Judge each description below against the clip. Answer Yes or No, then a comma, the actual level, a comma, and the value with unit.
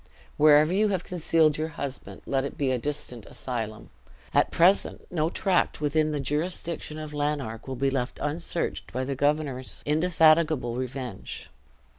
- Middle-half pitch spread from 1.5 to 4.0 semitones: Yes, average, 3.3 semitones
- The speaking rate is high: No, average, 150 wpm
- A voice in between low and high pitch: Yes, medium, 150 Hz